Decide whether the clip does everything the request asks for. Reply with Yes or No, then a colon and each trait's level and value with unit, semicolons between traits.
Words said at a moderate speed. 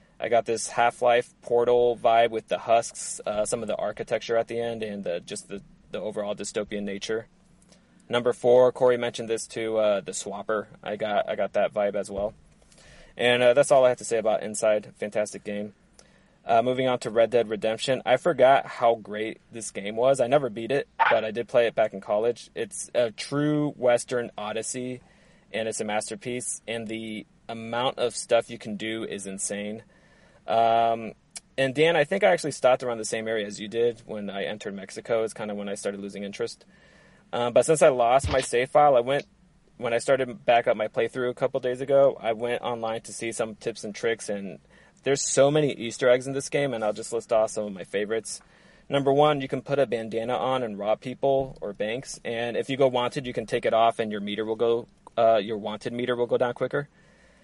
No: fast, 220 wpm